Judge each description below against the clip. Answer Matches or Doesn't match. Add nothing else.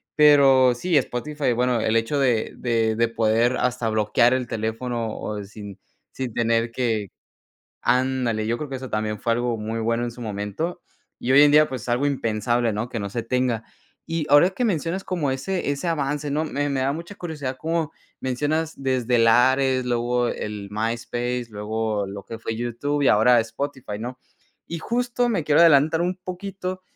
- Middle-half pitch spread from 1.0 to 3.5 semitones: Doesn't match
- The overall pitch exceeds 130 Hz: Doesn't match